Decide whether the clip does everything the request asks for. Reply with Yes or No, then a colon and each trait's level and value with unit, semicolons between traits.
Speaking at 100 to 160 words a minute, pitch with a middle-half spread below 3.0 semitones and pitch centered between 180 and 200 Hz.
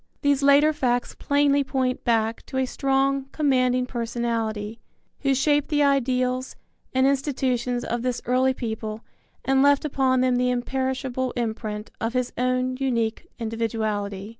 No: average, 140 wpm; narrow, 2.5 semitones; very high, 255 Hz